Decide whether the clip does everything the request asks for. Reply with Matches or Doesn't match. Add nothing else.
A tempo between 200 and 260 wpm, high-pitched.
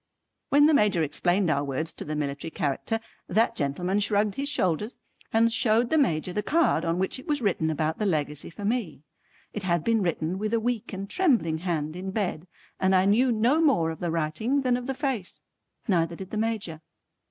Matches